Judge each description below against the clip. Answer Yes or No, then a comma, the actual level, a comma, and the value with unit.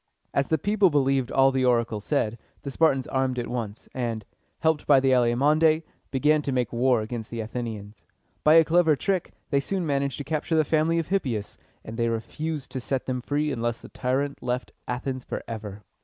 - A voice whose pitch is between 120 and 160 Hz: Yes, low, 135 Hz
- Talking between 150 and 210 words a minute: Yes, average, 190 wpm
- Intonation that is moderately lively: Yes, average, 4.3 semitones